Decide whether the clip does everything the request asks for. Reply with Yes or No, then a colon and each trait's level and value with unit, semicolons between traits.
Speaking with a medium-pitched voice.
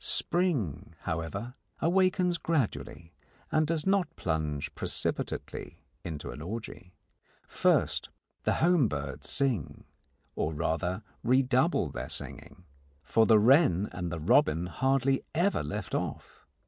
No: low, 110 Hz